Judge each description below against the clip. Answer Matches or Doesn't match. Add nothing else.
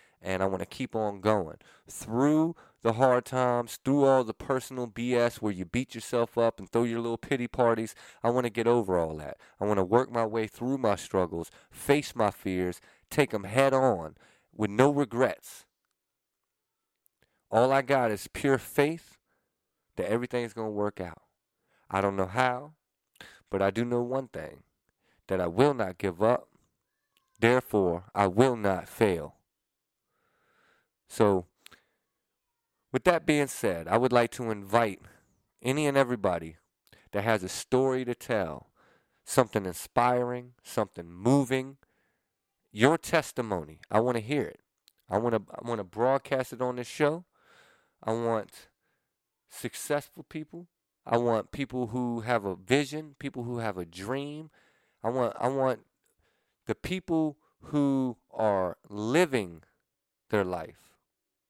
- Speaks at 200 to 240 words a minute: Doesn't match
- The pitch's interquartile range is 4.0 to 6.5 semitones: Matches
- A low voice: Matches